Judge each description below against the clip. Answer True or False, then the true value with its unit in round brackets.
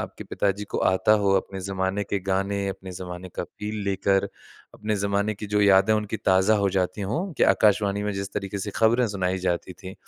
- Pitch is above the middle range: False (100 Hz)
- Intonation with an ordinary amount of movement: False (1.6 semitones)